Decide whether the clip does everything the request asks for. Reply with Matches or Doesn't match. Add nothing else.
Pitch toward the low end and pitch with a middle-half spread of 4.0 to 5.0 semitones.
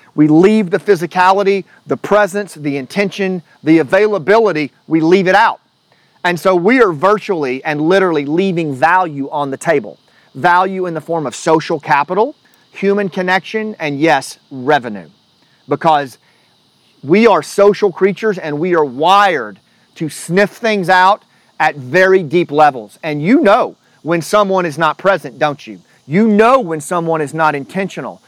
Doesn't match